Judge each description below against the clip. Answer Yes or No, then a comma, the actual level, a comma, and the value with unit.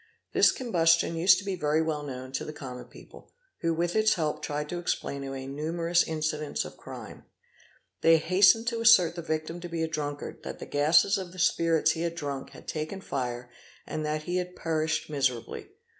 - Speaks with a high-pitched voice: No, medium, 160 Hz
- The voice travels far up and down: No, average, 2.8 semitones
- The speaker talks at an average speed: No, fast, 215 wpm